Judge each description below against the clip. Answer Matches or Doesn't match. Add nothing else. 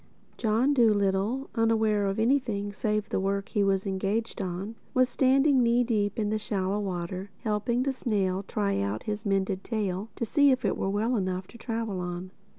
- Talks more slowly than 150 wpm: Doesn't match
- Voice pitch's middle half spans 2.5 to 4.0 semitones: Matches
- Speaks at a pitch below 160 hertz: Doesn't match